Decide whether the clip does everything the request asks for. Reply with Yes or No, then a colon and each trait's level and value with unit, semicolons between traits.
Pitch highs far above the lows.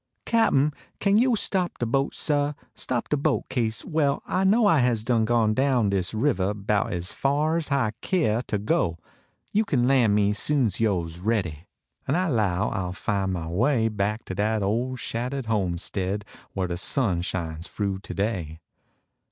Yes: wide, 6.2 semitones